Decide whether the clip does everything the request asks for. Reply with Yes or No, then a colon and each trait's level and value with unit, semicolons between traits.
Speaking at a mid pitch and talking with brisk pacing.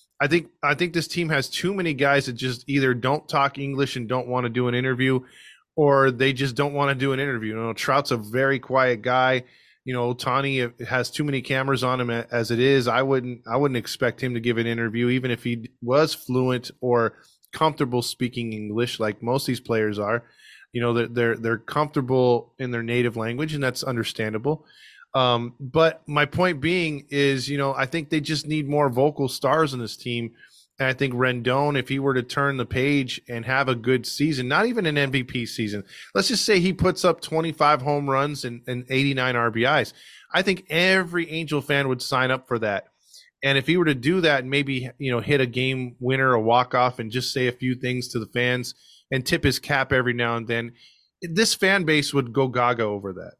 No: low, 130 Hz; fast, 220 wpm